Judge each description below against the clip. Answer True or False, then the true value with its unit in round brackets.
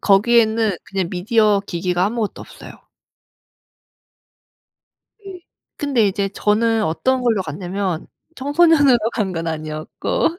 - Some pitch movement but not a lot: True (4.6 semitones)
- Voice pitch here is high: True (210 Hz)